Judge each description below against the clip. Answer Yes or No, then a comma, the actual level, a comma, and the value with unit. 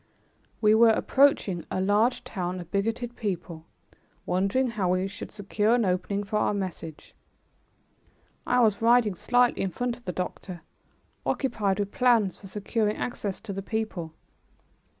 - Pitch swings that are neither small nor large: Yes, average, 3.6 semitones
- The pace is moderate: Yes, average, 150 wpm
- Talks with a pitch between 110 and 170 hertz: No, high, 205 Hz